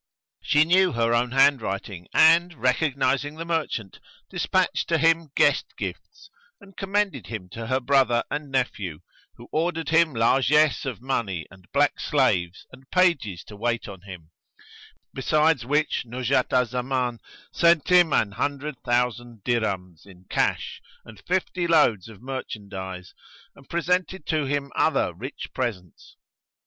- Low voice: Yes, low, 130 Hz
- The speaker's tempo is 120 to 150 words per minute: Yes, average, 140 wpm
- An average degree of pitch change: No, wide, 6.2 semitones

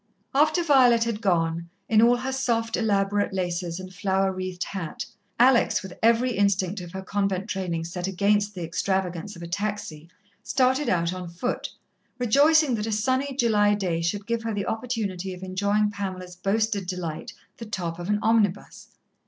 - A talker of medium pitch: No, high, 200 Hz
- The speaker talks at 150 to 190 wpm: Yes, average, 170 wpm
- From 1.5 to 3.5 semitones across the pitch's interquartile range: No, average, 3.9 semitones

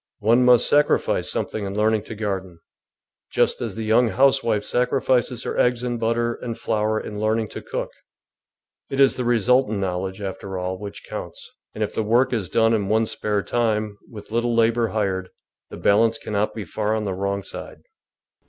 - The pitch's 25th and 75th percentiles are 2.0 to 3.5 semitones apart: Yes, narrow, 2.6 semitones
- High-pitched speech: No, low, 110 Hz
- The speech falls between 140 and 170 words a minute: No, average, 185 wpm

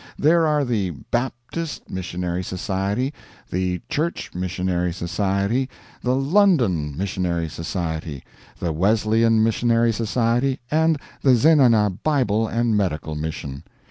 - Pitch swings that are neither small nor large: No, wide, 6.1 semitones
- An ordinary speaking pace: No, slow, 110 wpm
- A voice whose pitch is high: No, low, 105 Hz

